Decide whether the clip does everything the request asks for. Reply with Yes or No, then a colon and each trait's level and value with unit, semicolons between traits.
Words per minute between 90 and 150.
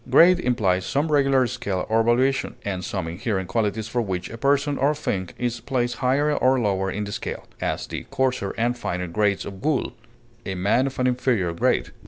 No: average, 195 wpm